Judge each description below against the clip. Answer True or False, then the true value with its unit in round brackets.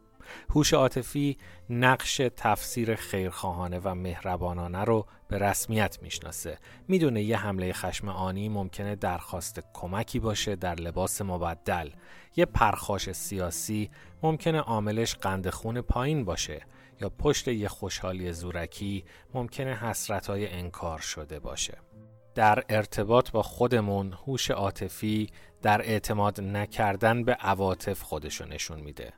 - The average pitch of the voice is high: False (100 Hz)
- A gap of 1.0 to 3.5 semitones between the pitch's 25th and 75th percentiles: False (4.0 semitones)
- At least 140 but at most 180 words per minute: False (115 wpm)